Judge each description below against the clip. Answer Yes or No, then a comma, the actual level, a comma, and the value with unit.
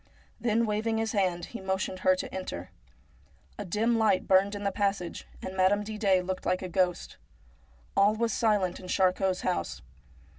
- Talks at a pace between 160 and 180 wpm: Yes, average, 170 wpm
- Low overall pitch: No, high, 190 Hz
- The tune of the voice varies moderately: No, narrow, 2.3 semitones